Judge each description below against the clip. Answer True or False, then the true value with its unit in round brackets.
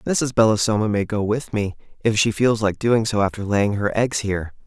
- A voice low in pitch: True (110 Hz)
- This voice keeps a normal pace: False (220 wpm)